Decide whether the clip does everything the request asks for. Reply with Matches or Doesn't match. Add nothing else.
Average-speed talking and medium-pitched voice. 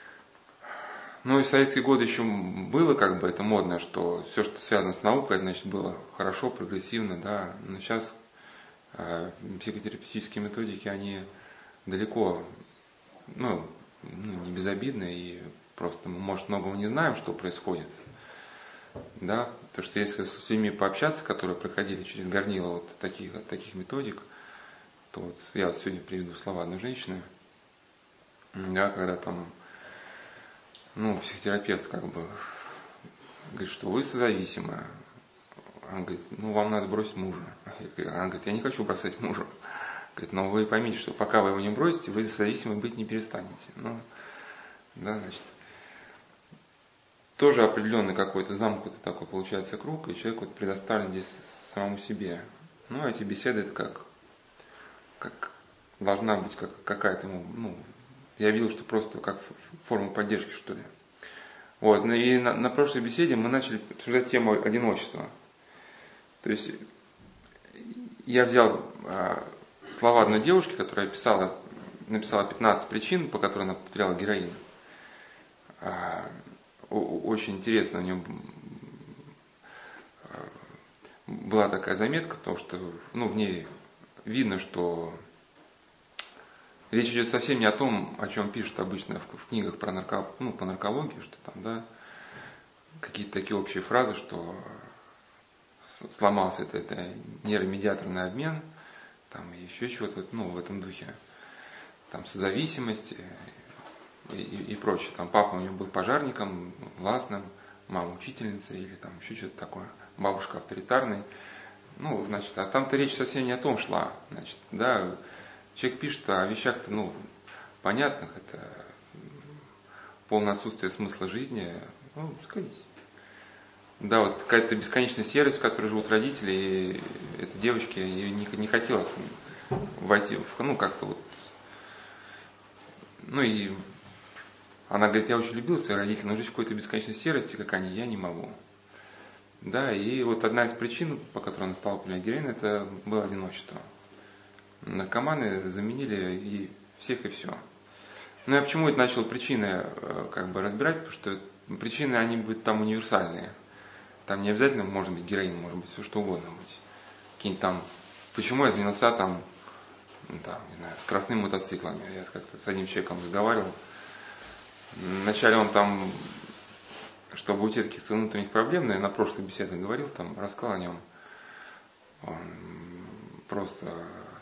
Doesn't match